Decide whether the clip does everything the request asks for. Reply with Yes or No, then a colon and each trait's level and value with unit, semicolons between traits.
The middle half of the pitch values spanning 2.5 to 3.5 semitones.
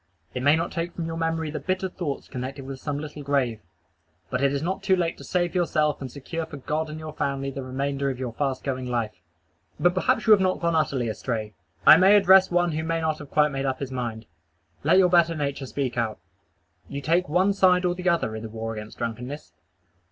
No: average, 4.7 semitones